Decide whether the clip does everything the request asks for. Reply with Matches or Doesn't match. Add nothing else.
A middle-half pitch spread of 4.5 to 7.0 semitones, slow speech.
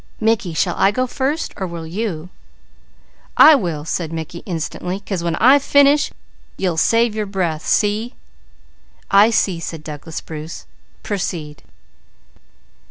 Matches